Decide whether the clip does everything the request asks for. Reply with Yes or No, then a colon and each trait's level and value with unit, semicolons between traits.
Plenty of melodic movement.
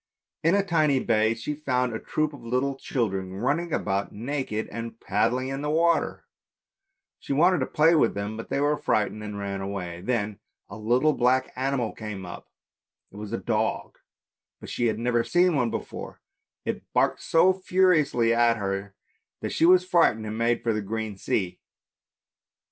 Yes: wide, 5.7 semitones